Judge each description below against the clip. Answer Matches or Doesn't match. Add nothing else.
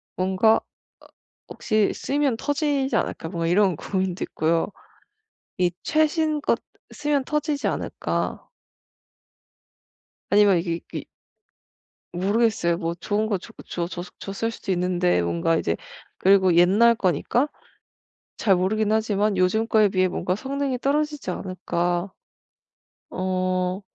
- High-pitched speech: Matches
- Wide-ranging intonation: Doesn't match